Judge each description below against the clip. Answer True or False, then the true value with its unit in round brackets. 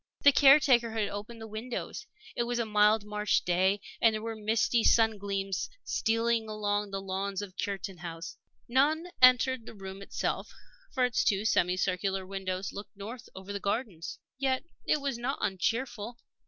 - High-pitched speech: True (210 Hz)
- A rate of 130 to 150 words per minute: False (170 wpm)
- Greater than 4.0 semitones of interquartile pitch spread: False (3.4 semitones)